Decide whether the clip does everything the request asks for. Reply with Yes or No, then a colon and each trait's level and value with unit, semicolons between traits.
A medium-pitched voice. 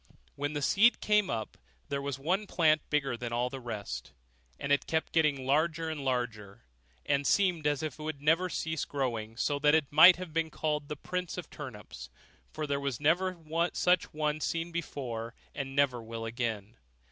Yes: medium, 145 Hz